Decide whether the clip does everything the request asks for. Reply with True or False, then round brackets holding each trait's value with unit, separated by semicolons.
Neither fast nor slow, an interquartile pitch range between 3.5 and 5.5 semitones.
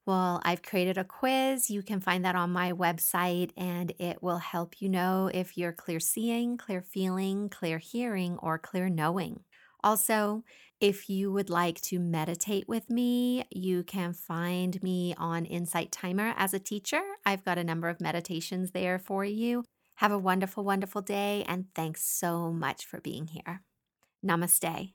False (170 wpm; 2.8 semitones)